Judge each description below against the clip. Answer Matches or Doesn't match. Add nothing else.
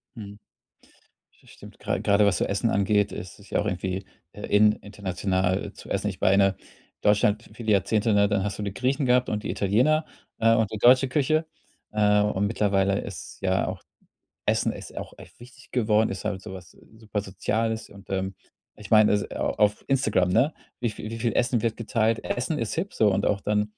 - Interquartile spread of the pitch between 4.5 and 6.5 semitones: Doesn't match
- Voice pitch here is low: Matches